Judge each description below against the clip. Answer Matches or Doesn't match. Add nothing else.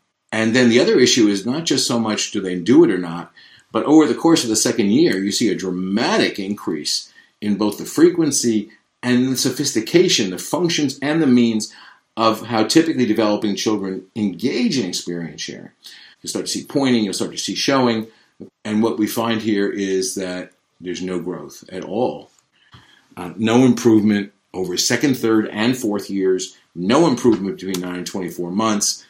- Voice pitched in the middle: Doesn't match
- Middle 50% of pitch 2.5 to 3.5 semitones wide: Doesn't match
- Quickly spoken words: Doesn't match